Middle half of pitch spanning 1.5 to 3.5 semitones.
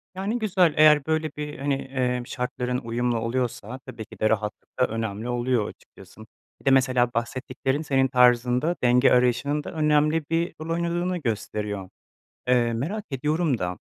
No: average, 4.1 semitones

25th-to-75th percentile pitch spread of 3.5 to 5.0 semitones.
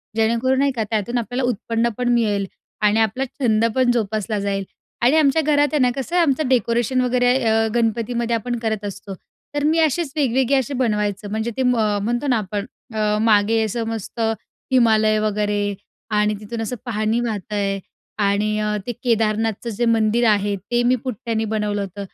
No: average, 2.8 semitones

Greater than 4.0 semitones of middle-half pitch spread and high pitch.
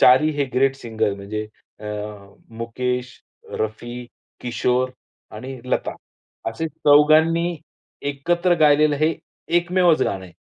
No: average, 5.0 semitones; low, 130 Hz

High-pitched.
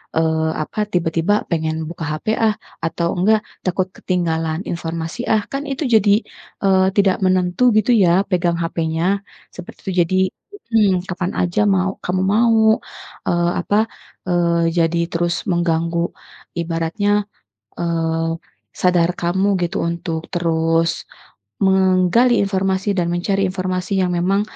No: medium, 180 Hz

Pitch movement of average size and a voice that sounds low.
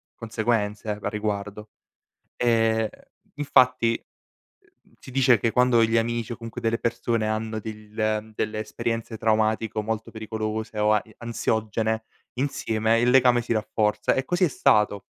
No: narrow, 1.5 semitones; low, 110 Hz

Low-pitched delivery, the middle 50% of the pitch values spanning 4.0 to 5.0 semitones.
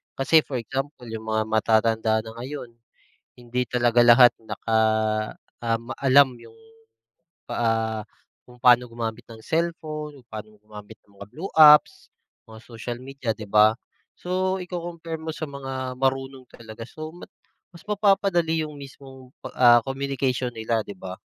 Yes: low, 125 Hz; average, 4.7 semitones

